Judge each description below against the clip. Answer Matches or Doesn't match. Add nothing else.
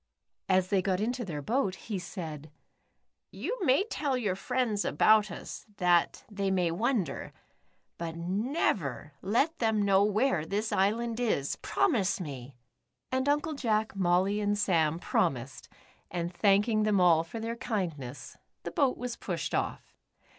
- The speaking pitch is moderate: Doesn't match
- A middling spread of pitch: Matches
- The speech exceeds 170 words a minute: Doesn't match